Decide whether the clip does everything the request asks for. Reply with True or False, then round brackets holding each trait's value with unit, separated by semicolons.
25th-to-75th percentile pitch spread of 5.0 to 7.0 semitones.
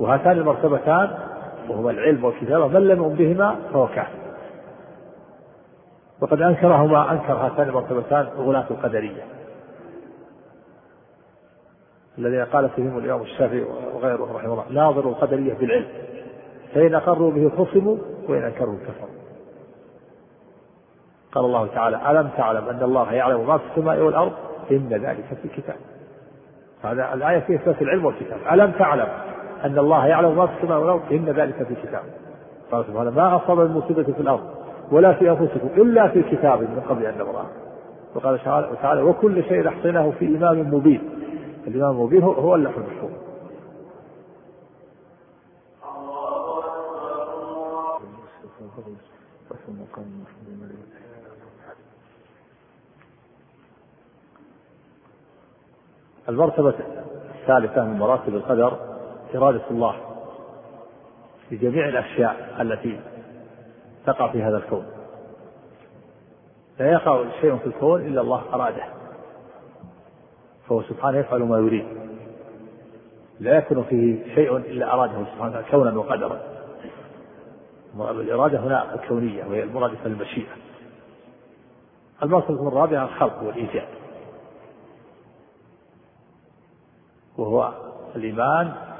True (5.4 semitones)